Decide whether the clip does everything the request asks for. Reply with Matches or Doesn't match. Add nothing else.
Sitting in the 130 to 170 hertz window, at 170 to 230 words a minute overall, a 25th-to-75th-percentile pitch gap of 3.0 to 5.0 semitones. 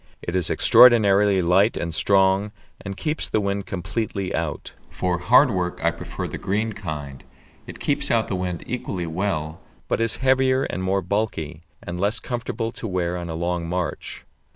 Doesn't match